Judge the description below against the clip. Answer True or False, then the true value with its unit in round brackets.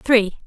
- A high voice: True (225 Hz)